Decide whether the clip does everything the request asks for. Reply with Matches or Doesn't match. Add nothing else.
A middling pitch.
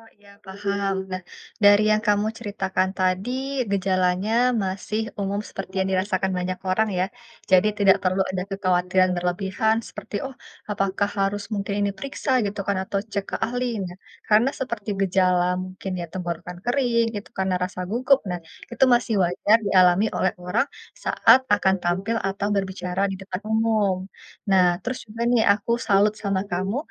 Doesn't match